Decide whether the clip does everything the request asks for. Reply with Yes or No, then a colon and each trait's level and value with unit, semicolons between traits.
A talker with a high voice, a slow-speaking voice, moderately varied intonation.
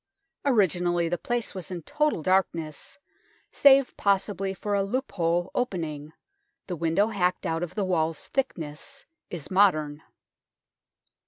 No: medium, 180 Hz; slow, 120 wpm; average, 3.8 semitones